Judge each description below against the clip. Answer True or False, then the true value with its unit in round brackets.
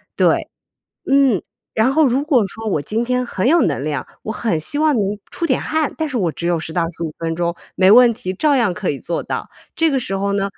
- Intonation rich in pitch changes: True (7.5 semitones)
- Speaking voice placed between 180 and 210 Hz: False (220 Hz)